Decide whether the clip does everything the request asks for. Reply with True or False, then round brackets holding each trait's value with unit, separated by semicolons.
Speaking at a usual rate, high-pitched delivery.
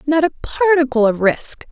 True (175 wpm; 285 Hz)